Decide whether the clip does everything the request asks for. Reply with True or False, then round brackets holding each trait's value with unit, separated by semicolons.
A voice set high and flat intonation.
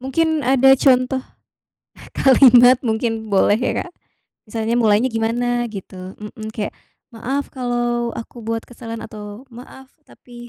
True (240 Hz; 2.3 semitones)